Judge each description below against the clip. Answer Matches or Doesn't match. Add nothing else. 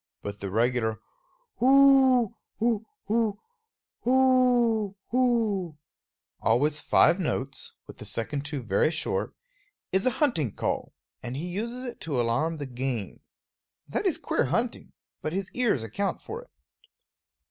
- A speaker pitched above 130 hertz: Matches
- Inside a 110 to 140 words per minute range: Matches